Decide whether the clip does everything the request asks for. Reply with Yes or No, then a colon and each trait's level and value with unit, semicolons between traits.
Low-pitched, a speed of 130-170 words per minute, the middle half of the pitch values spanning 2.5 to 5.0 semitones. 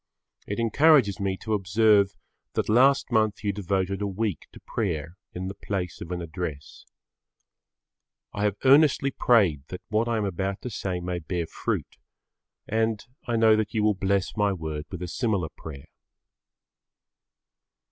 Yes: low, 100 Hz; average, 155 wpm; average, 3.5 semitones